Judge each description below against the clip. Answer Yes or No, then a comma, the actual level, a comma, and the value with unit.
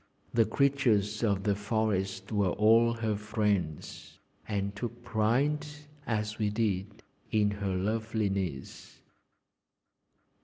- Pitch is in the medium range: No, low, 105 Hz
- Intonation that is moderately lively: No, narrow, 2.2 semitones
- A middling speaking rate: No, slow, 105 wpm